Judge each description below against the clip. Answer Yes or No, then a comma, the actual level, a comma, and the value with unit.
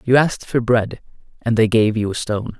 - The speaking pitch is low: Yes, low, 115 Hz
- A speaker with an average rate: No, fast, 230 wpm